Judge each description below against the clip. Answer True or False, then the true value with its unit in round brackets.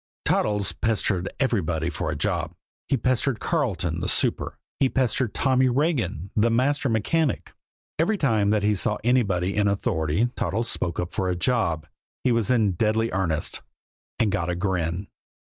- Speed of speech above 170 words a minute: False (160 wpm)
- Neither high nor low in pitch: False (105 Hz)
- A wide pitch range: True (5.8 semitones)